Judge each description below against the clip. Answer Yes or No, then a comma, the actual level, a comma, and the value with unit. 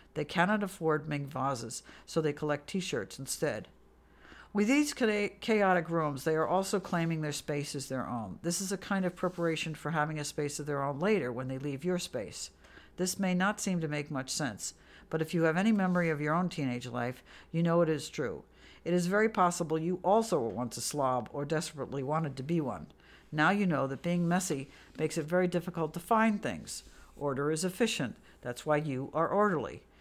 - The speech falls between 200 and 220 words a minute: Yes, fast, 205 wpm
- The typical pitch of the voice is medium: Yes, medium, 160 Hz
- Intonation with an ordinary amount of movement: Yes, average, 4.2 semitones